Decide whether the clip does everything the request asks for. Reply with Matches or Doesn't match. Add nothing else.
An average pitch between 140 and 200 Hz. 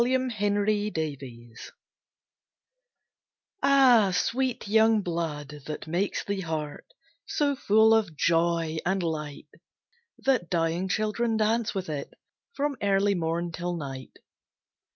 Matches